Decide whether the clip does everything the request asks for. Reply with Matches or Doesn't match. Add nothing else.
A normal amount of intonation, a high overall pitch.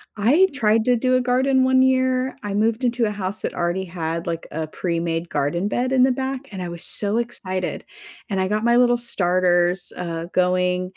Doesn't match